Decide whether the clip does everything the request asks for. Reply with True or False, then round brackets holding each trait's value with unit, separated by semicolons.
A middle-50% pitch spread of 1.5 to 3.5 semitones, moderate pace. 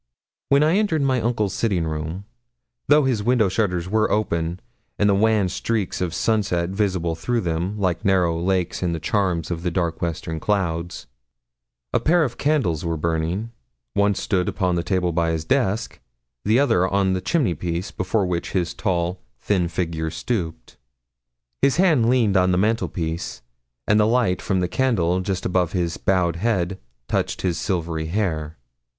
False (4.1 semitones; 165 wpm)